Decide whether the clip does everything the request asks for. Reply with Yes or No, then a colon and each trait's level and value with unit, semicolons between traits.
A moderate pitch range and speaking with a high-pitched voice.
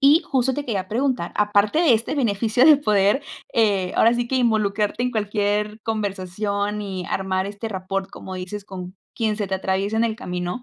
Yes: average, 3.2 semitones; high, 210 Hz